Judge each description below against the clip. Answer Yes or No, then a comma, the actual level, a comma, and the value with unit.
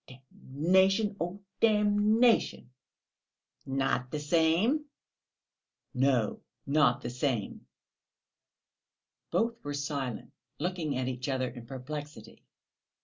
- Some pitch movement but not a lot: No, wide, 6.6 semitones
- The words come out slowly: Yes, slow, 85 wpm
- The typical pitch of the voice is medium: Yes, medium, 145 Hz